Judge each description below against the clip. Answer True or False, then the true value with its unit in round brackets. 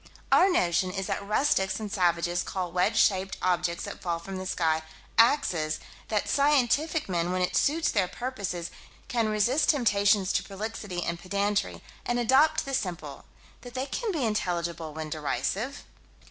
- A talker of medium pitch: False (195 Hz)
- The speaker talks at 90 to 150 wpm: False (160 wpm)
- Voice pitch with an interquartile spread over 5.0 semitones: True (5.6 semitones)